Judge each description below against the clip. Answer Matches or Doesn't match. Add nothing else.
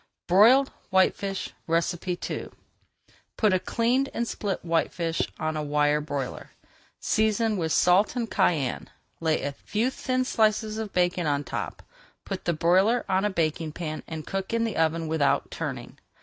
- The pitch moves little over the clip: Doesn't match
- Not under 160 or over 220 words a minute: Doesn't match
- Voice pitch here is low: Doesn't match